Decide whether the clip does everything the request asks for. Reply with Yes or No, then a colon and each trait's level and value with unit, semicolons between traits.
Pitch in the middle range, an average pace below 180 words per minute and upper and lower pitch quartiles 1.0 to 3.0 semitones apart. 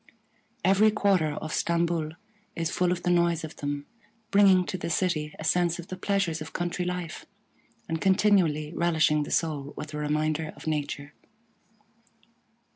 Yes: medium, 165 Hz; average, 155 wpm; average, 2.7 semitones